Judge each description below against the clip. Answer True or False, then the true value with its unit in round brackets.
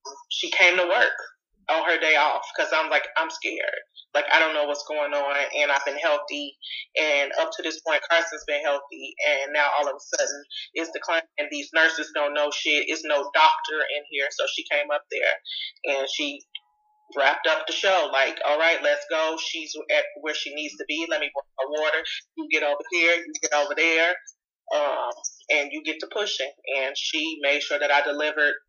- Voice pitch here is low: False (160 Hz)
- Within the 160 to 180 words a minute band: False (205 wpm)